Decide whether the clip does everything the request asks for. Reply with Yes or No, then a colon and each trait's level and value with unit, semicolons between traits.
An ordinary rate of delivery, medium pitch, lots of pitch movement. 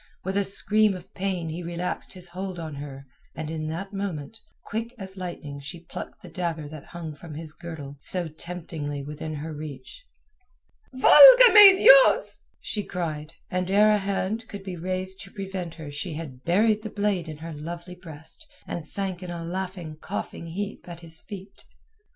No: average, 180 wpm; medium, 175 Hz; average, 3.7 semitones